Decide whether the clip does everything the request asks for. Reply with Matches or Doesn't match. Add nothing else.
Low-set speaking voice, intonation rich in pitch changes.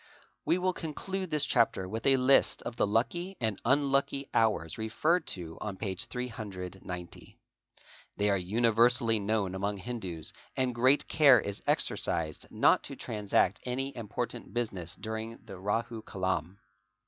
Doesn't match